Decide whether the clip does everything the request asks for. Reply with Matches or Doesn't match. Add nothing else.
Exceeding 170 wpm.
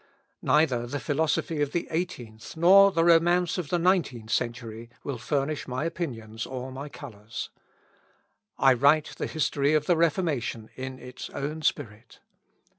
Doesn't match